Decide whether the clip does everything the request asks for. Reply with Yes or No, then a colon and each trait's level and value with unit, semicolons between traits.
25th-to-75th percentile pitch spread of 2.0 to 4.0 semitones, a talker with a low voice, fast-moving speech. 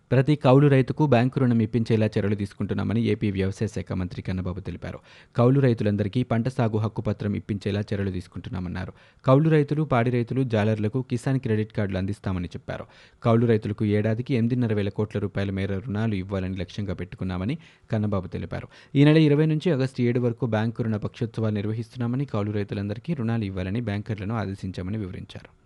Yes: average, 3.5 semitones; low, 110 Hz; fast, 150 wpm